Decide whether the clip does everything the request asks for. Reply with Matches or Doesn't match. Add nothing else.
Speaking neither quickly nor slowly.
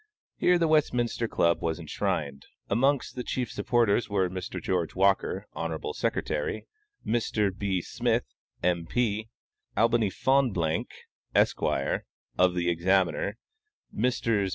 Doesn't match